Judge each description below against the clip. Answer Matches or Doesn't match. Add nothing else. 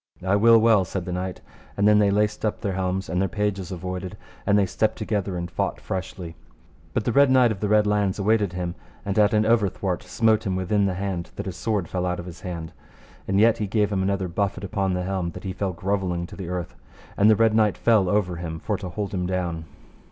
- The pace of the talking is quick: Matches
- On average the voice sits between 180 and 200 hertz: Doesn't match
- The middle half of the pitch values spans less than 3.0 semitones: Matches